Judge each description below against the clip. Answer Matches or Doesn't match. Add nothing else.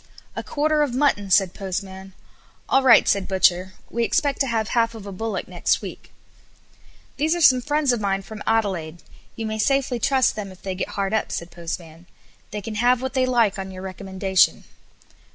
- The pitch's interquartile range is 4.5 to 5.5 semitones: Matches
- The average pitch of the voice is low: Doesn't match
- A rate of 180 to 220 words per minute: Matches